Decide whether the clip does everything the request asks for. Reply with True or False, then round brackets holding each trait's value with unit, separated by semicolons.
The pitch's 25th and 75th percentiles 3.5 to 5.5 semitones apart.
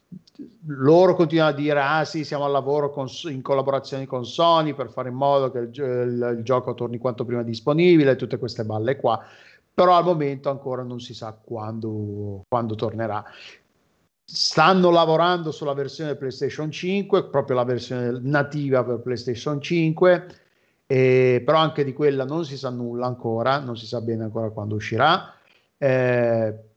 True (4.0 semitones)